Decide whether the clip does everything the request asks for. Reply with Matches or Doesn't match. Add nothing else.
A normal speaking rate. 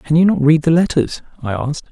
Doesn't match